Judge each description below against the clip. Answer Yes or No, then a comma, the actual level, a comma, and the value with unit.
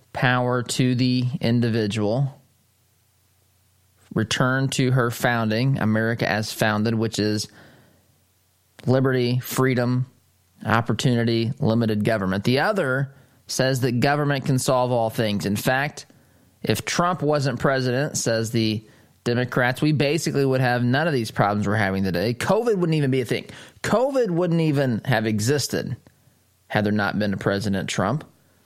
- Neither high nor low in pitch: No, low, 120 Hz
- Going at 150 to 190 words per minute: No, slow, 135 wpm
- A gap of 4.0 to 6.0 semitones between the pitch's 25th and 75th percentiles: No, average, 3.6 semitones